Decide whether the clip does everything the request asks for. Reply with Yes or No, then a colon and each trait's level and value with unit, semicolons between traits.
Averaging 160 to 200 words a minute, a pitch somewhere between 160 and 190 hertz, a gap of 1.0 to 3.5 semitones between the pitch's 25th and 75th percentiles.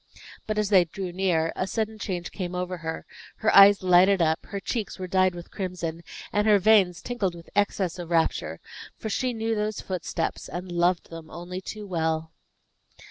Yes: average, 185 wpm; medium, 185 Hz; average, 2.9 semitones